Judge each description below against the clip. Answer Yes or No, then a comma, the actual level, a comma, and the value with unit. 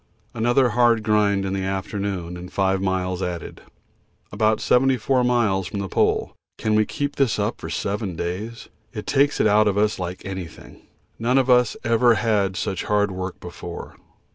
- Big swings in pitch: No, average, 3.4 semitones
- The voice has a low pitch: Yes, low, 105 Hz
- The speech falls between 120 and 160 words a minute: No, average, 170 wpm